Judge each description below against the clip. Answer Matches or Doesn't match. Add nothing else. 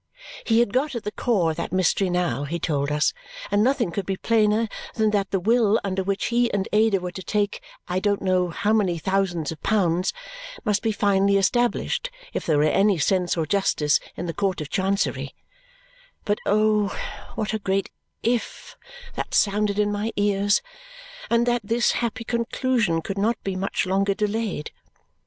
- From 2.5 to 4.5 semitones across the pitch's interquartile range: Matches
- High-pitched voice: Matches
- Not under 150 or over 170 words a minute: Doesn't match